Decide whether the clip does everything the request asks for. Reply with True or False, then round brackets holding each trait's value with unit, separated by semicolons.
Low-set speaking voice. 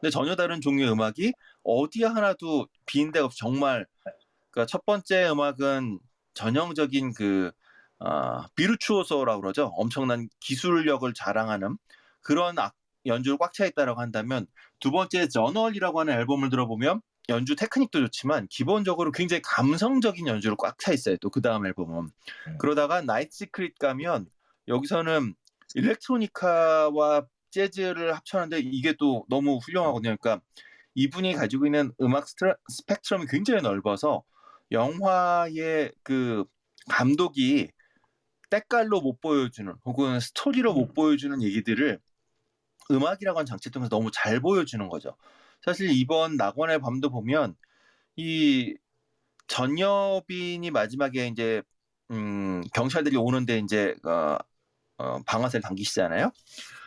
False (145 Hz)